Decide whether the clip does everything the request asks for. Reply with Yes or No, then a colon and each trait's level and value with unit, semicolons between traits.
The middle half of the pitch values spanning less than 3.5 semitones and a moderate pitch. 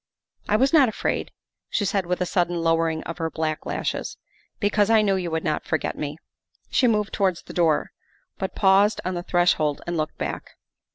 No: average, 3.9 semitones; medium, 180 Hz